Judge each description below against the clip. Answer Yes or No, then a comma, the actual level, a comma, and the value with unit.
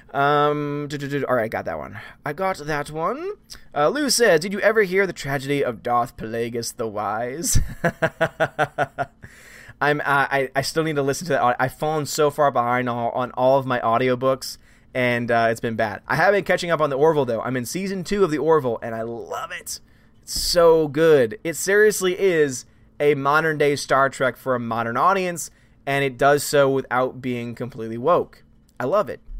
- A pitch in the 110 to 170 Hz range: Yes, medium, 140 Hz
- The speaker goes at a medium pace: No, fast, 210 wpm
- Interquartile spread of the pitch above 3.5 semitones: Yes, average, 4.7 semitones